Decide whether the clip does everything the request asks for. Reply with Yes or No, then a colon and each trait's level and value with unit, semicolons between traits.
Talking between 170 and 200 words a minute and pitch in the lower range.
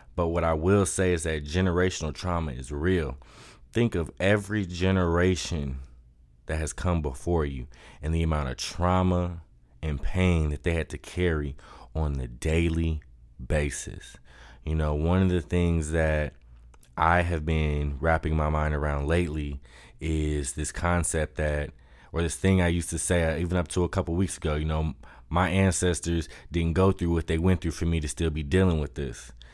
Yes: average, 180 wpm; very low, 80 Hz